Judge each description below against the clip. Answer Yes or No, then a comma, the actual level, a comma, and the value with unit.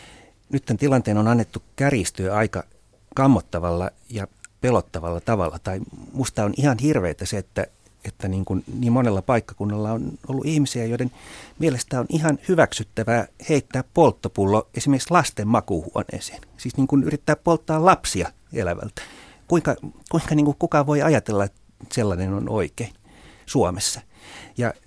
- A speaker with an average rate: Yes, average, 140 wpm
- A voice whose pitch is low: Yes, low, 120 Hz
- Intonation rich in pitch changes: Yes, wide, 5.7 semitones